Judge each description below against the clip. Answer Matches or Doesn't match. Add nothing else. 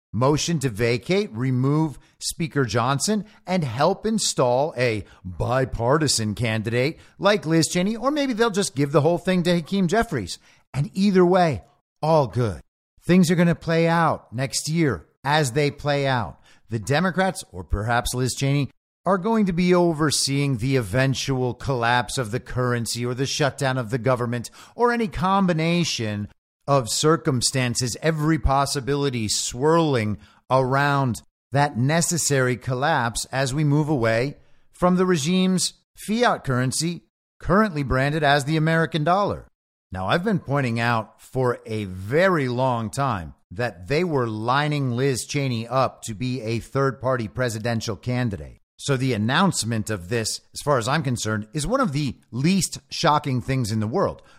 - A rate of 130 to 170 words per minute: Matches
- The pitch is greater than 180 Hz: Doesn't match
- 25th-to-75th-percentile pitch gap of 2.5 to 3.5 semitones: Doesn't match